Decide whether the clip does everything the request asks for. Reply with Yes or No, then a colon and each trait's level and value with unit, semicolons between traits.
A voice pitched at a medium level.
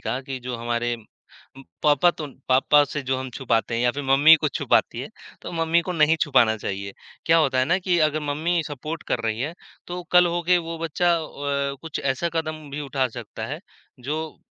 Yes: medium, 150 Hz